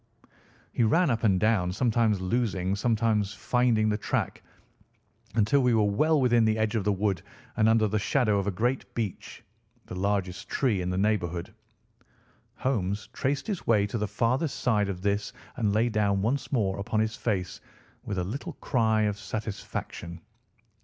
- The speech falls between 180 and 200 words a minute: No, average, 170 wpm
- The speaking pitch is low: Yes, low, 110 Hz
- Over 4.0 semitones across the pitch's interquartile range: No, average, 2.8 semitones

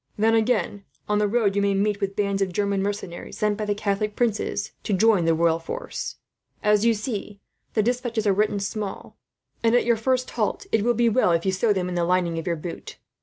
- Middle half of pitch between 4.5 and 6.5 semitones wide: No, narrow, 2.4 semitones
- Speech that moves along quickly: Yes, fast, 225 wpm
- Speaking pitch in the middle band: No, high, 205 Hz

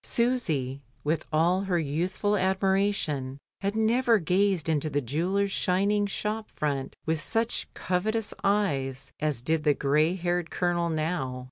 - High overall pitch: No, medium, 175 Hz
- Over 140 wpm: No, slow, 135 wpm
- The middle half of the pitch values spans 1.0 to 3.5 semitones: No, average, 5.0 semitones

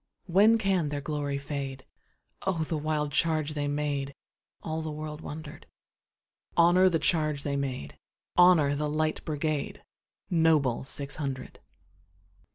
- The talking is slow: Yes, slow, 105 wpm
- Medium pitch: Yes, medium, 150 Hz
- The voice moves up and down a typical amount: No, narrow, 2.1 semitones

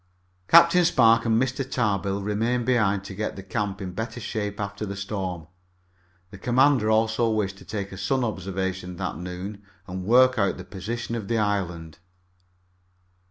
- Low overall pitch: Yes, low, 105 Hz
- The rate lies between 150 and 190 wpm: Yes, average, 160 wpm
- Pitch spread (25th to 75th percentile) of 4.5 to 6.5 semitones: No, average, 3.3 semitones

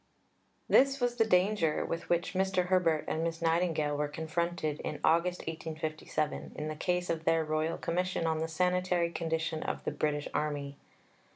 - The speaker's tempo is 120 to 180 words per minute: Yes, average, 165 wpm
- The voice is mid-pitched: Yes, medium, 165 Hz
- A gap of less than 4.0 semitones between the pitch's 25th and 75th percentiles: Yes, narrow, 2.4 semitones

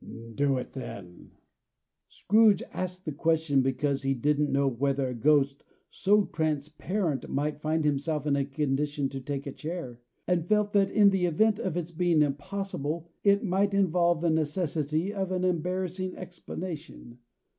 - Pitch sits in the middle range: Yes, medium, 155 Hz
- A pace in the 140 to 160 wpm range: Yes, average, 155 wpm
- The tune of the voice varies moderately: Yes, average, 4.7 semitones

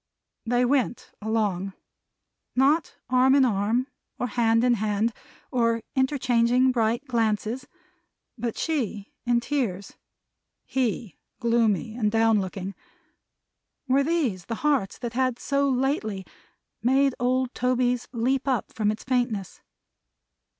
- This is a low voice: No, high, 240 Hz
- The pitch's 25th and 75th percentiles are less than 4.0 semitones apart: Yes, average, 3.0 semitones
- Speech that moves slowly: Yes, slow, 115 wpm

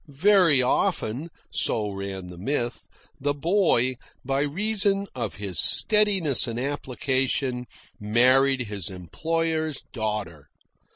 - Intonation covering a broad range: Yes, wide, 6.7 semitones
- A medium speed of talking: No, slow, 105 wpm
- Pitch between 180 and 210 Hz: No, low, 130 Hz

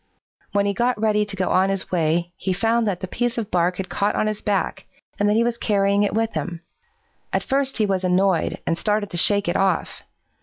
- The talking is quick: Yes, fast, 230 wpm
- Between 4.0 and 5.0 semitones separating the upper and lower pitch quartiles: No, average, 2.7 semitones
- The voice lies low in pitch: No, high, 200 Hz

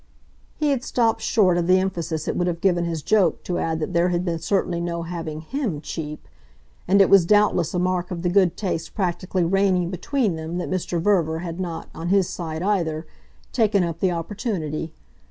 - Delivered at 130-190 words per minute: No, average, 200 wpm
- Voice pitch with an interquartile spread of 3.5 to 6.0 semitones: No, average, 2.7 semitones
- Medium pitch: Yes, medium, 175 Hz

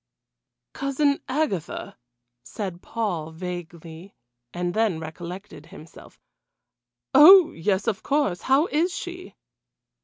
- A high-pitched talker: Yes, high, 195 Hz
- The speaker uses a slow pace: Yes, slow, 95 wpm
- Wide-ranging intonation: Yes, wide, 8.6 semitones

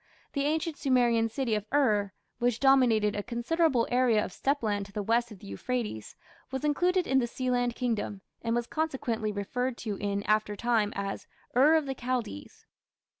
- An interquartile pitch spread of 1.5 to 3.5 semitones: No, average, 4.1 semitones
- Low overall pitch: No, high, 240 Hz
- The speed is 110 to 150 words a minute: No, average, 175 wpm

